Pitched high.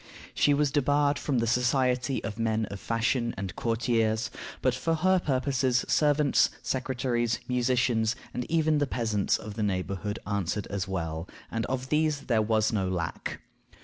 No: low, 120 Hz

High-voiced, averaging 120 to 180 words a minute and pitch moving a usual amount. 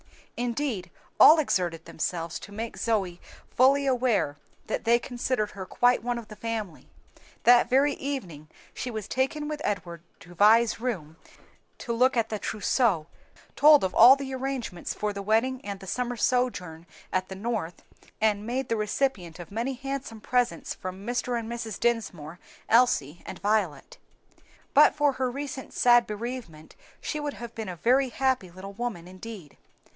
Yes: high, 230 Hz; average, 160 wpm; average, 5.0 semitones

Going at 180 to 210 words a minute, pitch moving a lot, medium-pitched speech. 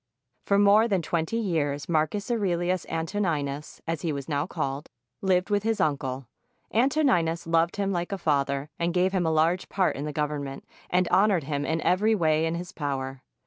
No: average, 190 wpm; average, 4.3 semitones; medium, 165 Hz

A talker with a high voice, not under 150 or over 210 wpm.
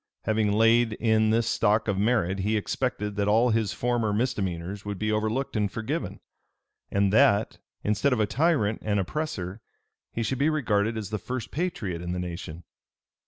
No: low, 110 Hz; average, 170 wpm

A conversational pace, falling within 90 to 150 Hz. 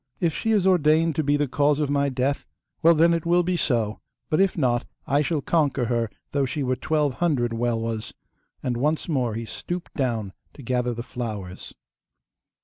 Yes: average, 190 wpm; medium, 140 Hz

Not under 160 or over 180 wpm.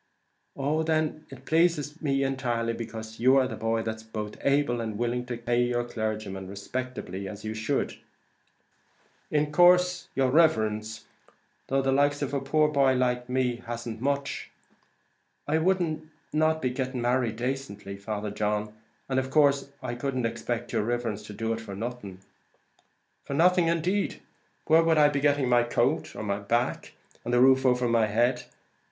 Yes: average, 170 wpm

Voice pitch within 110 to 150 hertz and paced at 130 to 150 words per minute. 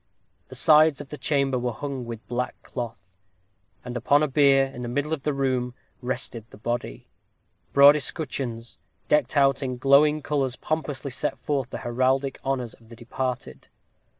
No: low, 135 Hz; average, 165 wpm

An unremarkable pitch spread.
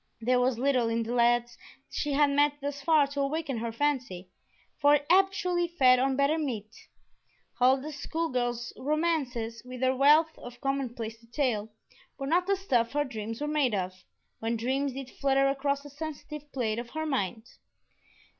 Yes: average, 3.6 semitones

